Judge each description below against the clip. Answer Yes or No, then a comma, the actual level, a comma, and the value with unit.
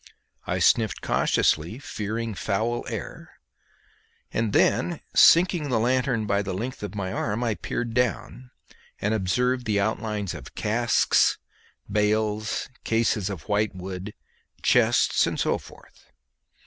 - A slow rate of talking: Yes, slow, 125 wpm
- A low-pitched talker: Yes, low, 110 Hz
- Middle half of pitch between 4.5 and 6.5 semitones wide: No, average, 2.8 semitones